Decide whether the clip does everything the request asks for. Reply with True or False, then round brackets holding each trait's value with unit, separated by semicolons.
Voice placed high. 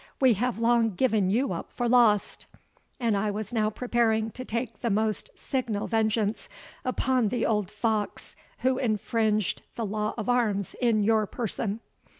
True (220 Hz)